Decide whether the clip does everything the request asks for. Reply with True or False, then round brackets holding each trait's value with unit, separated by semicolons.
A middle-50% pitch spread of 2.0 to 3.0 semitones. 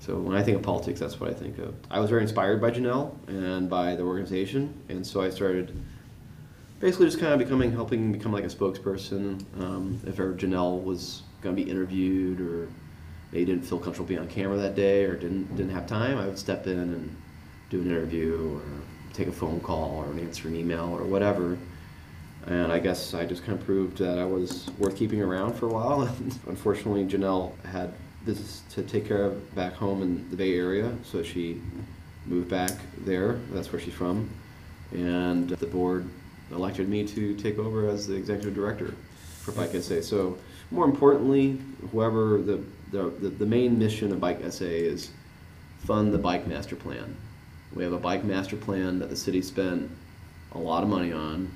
True (2.5 semitones)